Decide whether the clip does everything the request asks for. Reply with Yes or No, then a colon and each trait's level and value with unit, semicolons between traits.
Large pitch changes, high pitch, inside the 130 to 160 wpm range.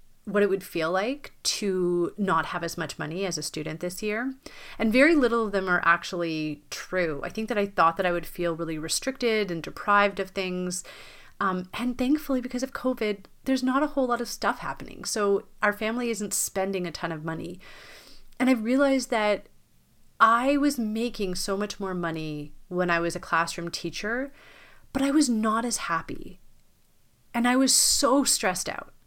No: wide, 5.8 semitones; high, 205 Hz; average, 190 wpm